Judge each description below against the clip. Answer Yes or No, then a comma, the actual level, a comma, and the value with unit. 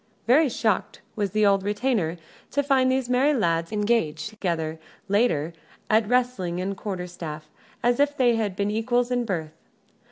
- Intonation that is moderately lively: No, wide, 5.7 semitones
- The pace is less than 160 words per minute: No, average, 165 wpm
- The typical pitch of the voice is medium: No, high, 210 Hz